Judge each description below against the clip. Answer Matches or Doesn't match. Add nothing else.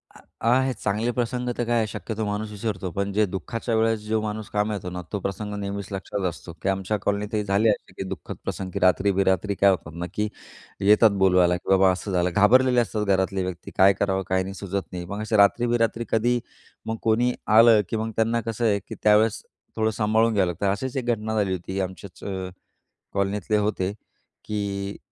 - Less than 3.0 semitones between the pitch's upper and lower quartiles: Matches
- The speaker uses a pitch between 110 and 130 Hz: Doesn't match